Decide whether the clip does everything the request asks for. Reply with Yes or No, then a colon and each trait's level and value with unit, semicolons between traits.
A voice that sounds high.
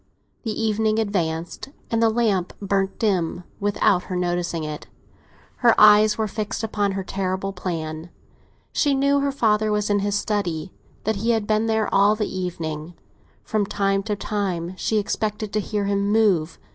Yes: high, 205 Hz